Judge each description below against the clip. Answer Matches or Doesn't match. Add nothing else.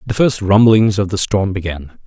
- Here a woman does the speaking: Doesn't match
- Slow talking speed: Doesn't match